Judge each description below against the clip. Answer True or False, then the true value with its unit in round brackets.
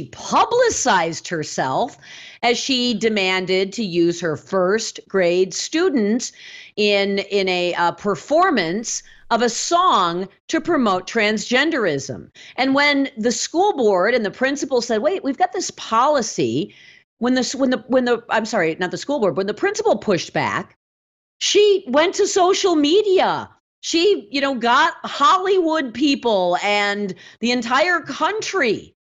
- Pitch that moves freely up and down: True (8.2 semitones)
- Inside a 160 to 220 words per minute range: False (140 wpm)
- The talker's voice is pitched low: False (245 Hz)